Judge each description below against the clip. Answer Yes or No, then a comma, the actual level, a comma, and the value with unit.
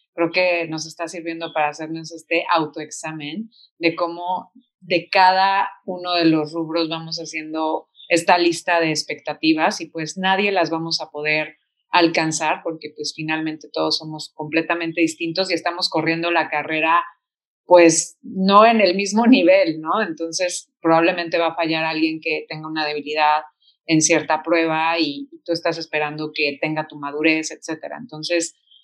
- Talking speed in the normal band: Yes, average, 150 wpm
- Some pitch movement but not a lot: No, narrow, 1.7 semitones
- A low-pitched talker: No, medium, 165 Hz